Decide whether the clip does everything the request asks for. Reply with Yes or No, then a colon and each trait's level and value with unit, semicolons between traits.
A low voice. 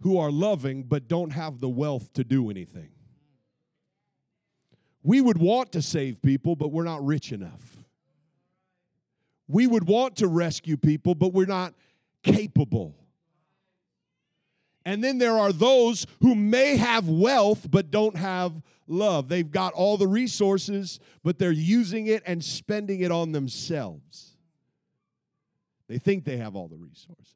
No: medium, 170 Hz